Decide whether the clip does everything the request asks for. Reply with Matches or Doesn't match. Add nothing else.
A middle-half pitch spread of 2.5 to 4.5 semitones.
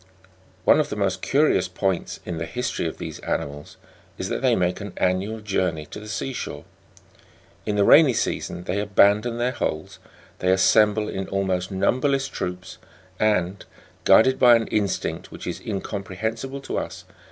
Matches